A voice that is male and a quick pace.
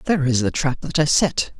Yes: male; fast, 265 wpm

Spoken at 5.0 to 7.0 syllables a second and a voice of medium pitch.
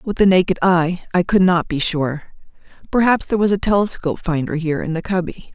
Yes: 6.0 syllables/s; medium, 180 Hz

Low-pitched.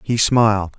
Yes: low, 110 Hz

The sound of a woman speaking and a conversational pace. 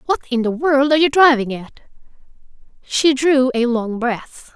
Yes: female; average, 170 wpm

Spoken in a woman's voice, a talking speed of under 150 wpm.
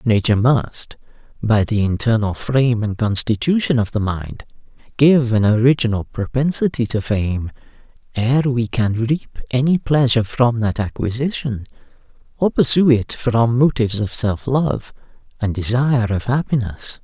No: male; slow, 135 wpm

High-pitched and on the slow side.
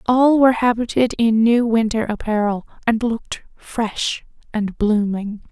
Yes: high, 225 Hz; slow, 130 wpm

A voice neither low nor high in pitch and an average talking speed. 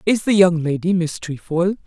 Yes: medium, 175 Hz; average, 195 wpm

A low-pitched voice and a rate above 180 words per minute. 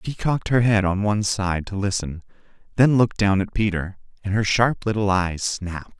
Yes: low, 100 Hz; average, 200 wpm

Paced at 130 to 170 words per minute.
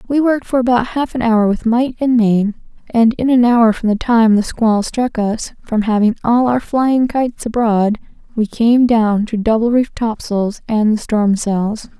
No: fast, 205 wpm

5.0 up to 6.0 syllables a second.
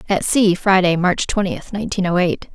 Yes: 5.1 syllables/s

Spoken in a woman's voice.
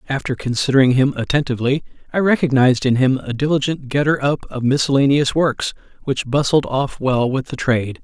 No: male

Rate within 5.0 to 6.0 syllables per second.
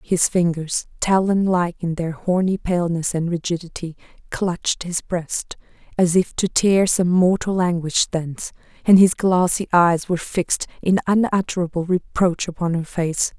No: 4.6 syllables/s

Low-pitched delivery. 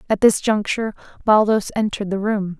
No: high, 210 Hz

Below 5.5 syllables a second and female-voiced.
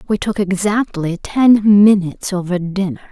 Yes: 4.6 syllables/s; female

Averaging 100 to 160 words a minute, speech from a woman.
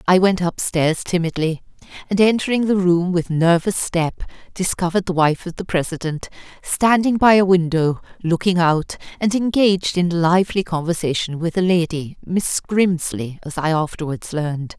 Yes: average, 155 wpm; female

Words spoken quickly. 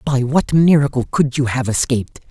No: average, 180 wpm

